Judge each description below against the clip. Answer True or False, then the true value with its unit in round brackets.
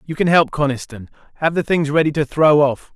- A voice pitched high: False (150 Hz)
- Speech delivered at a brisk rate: True (225 wpm)